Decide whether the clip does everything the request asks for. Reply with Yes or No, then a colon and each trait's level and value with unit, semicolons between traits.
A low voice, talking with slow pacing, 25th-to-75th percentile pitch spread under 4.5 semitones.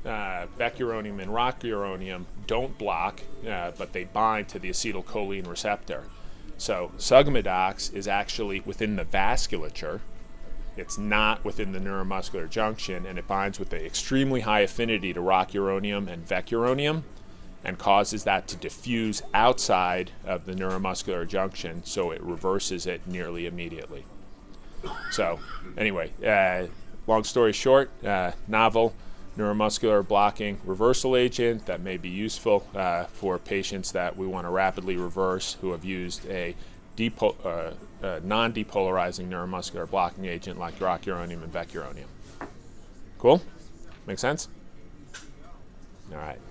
Yes: very low, 95 Hz; slow, 130 wpm; average, 2.7 semitones